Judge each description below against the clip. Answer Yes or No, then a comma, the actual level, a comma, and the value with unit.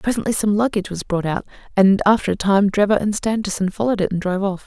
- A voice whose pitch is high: Yes, high, 200 Hz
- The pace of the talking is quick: Yes, fast, 230 wpm